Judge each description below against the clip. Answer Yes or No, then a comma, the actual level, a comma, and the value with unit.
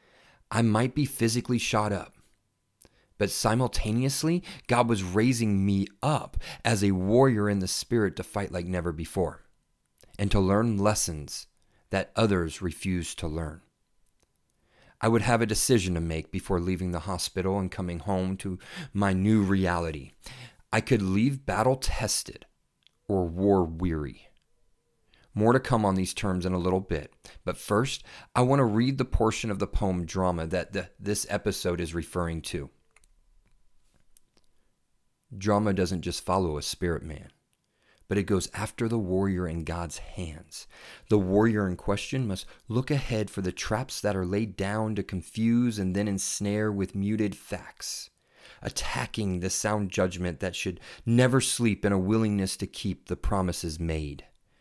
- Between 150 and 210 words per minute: Yes, average, 155 wpm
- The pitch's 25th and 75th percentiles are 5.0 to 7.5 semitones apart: No, average, 3.5 semitones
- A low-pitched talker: Yes, low, 100 Hz